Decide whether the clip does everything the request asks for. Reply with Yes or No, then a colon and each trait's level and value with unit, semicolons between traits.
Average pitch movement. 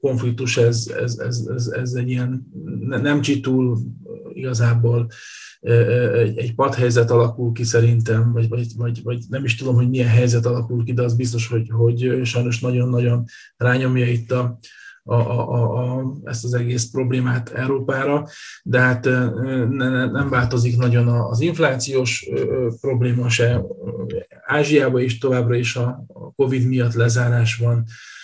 No: narrow, 1.3 semitones